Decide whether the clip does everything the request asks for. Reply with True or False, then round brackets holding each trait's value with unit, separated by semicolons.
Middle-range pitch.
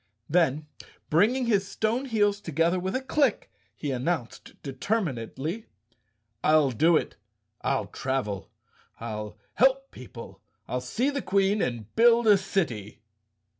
True (175 Hz)